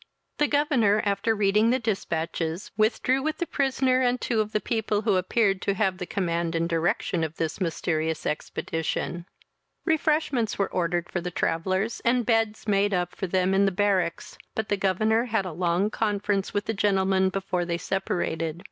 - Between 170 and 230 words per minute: Yes, average, 175 wpm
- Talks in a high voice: Yes, high, 195 Hz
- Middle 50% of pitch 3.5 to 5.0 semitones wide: Yes, average, 4.0 semitones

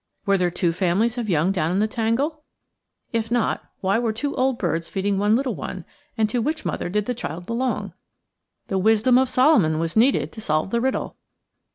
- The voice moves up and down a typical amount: Yes, average, 4.7 semitones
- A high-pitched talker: Yes, high, 220 Hz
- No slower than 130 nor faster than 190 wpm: No, average, 200 wpm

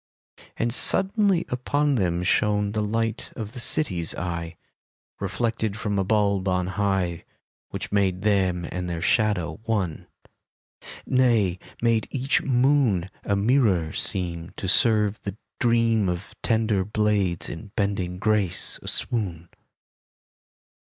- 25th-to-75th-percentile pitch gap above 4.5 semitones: No, average, 3.8 semitones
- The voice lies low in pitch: Yes, low, 105 Hz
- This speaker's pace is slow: Yes, slow, 125 wpm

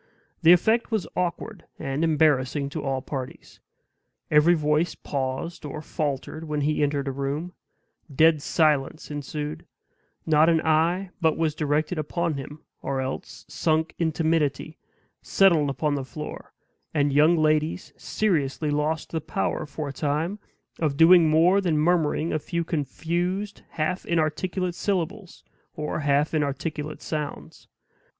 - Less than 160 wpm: Yes, slow, 135 wpm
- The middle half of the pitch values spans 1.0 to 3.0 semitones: Yes, narrow, 2.4 semitones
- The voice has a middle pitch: Yes, medium, 155 Hz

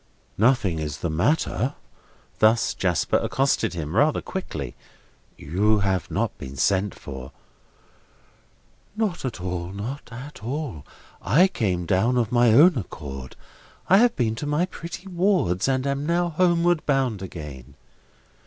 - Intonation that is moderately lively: No, wide, 8.9 semitones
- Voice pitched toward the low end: Yes, low, 115 Hz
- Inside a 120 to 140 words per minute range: Yes, slow, 135 wpm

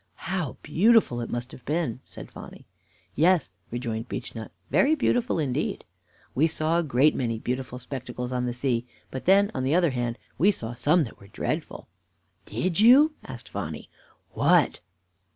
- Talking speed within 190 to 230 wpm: No, average, 160 wpm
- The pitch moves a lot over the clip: Yes, wide, 6.1 semitones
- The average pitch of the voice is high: No, low, 130 Hz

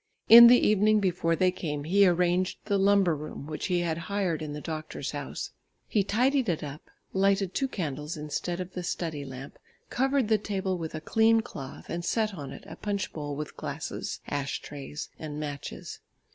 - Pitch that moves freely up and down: No, average, 4.9 semitones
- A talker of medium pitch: Yes, medium, 175 Hz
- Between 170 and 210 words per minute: Yes, average, 185 wpm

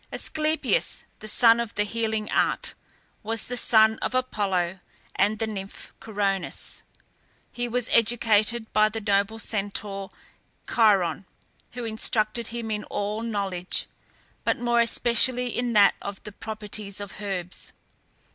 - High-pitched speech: Yes, high, 215 Hz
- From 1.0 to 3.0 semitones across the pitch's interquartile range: Yes, narrow, 2.5 semitones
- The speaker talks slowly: Yes, slow, 130 wpm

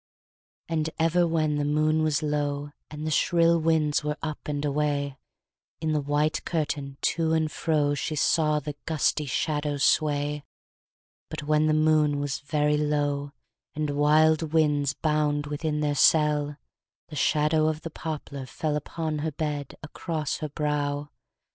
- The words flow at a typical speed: Yes, average, 150 wpm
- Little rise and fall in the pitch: Yes, narrow, 1.2 semitones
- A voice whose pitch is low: No, medium, 150 Hz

